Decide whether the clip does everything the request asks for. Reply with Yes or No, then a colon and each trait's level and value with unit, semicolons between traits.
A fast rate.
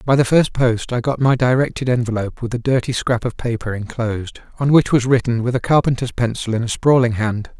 Yes: fast, 220 wpm